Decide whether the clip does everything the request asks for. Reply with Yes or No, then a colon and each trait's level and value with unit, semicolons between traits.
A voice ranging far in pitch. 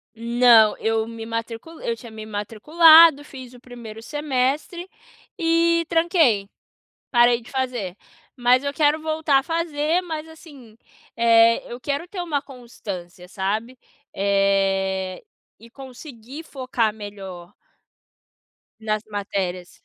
Yes: wide, 5.7 semitones